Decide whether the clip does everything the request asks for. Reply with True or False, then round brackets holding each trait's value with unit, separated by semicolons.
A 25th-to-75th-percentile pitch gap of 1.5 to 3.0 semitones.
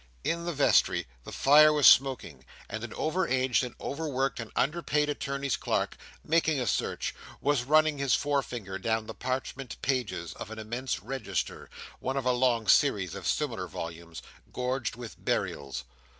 False (4.0 semitones)